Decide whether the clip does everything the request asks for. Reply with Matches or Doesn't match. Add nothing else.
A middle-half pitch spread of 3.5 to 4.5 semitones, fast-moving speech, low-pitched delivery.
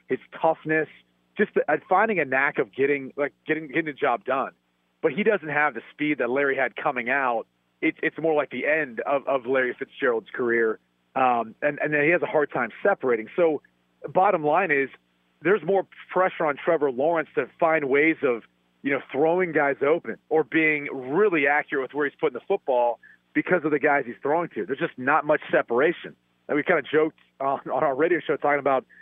Doesn't match